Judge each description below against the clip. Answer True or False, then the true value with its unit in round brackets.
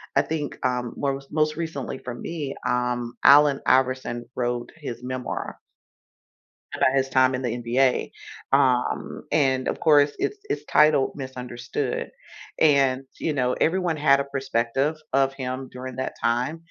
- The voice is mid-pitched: False (130 Hz)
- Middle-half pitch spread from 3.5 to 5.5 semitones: False (2.4 semitones)